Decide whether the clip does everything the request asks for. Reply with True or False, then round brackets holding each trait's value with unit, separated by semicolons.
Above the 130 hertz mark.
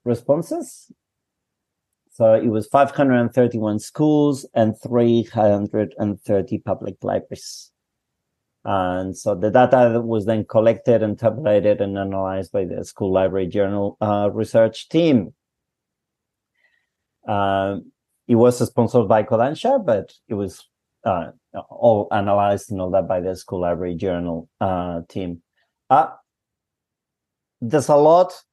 False (105 Hz)